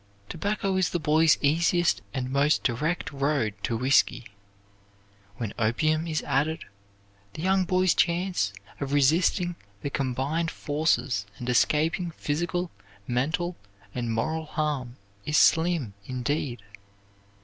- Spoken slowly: Yes, slow, 115 wpm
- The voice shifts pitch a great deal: No, average, 4.8 semitones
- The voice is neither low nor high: Yes, medium, 150 Hz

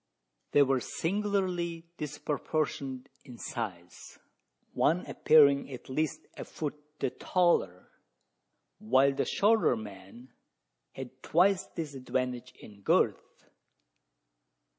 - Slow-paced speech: Yes, slow, 95 wpm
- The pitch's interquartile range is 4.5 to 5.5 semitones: Yes, average, 4.9 semitones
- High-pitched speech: No, medium, 140 Hz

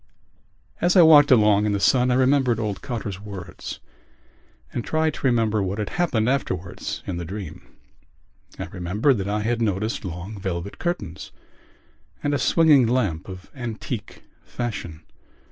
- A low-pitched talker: Yes, low, 110 Hz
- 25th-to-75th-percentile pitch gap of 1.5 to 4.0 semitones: No, average, 5.0 semitones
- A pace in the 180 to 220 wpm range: No, average, 150 wpm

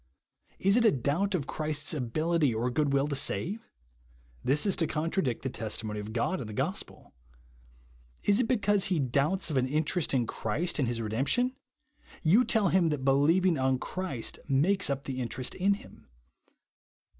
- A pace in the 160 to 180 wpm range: Yes, average, 175 wpm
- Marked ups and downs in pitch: Yes, wide, 6.3 semitones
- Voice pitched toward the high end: No, medium, 150 Hz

